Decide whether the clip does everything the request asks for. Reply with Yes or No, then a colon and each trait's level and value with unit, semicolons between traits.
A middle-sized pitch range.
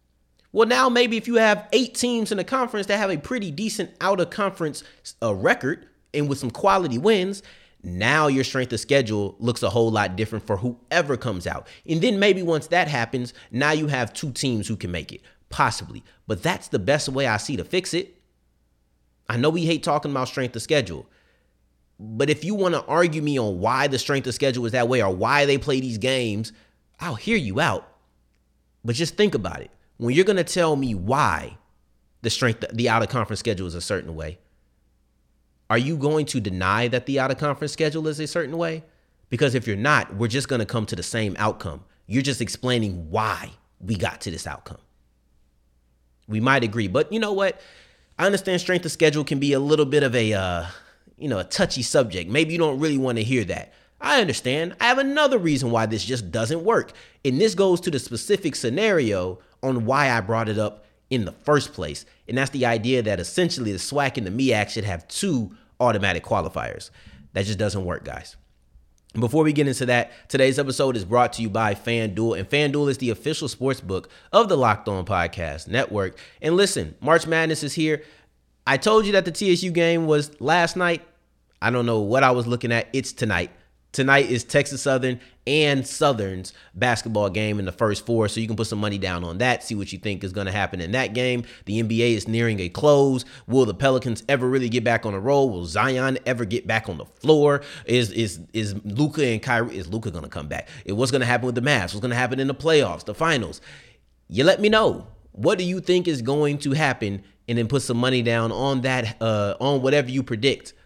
No: wide, 6.0 semitones